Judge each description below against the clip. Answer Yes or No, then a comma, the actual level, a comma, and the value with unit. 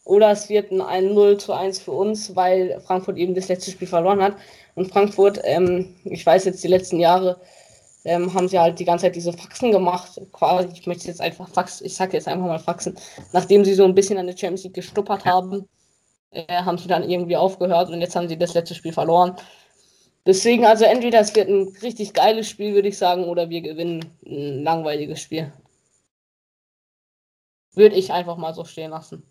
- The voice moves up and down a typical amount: No, narrow, 2.2 semitones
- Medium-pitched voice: Yes, medium, 180 Hz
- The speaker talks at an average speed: No, fast, 200 wpm